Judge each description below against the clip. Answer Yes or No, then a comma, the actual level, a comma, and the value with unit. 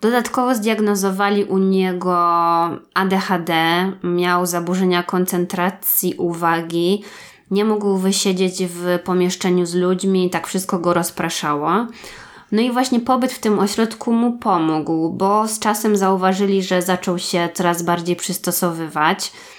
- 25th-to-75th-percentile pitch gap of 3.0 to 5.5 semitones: No, narrow, 2.5 semitones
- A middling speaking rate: Yes, average, 120 wpm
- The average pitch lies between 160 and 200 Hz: Yes, medium, 185 Hz